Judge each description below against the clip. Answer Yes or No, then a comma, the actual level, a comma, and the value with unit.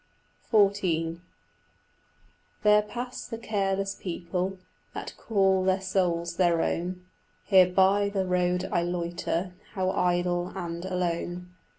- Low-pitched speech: No, medium, 185 Hz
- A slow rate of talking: Yes, slow, 110 wpm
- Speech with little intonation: Yes, narrow, 1.8 semitones